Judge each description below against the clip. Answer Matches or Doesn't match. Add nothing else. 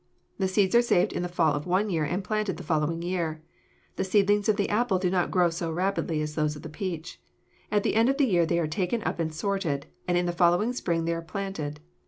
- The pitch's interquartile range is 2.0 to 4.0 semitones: Matches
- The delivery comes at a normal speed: Doesn't match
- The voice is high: Doesn't match